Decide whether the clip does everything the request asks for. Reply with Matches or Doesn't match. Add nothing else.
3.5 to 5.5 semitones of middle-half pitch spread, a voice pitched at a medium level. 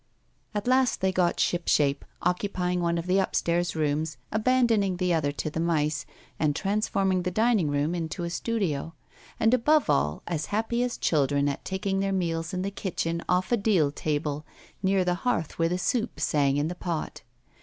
Matches